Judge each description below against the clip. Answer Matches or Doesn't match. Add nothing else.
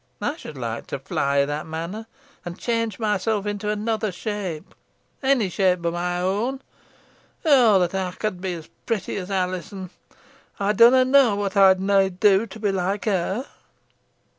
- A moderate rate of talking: Matches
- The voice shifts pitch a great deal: Doesn't match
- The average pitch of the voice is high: Matches